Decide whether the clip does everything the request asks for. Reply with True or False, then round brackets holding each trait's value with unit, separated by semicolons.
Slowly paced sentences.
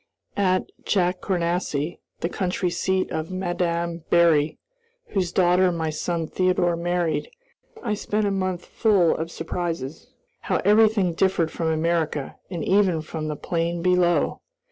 True (130 wpm)